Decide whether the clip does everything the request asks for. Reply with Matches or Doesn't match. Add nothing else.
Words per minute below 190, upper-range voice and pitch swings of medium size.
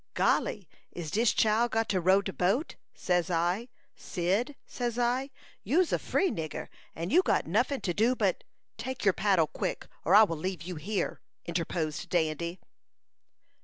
Doesn't match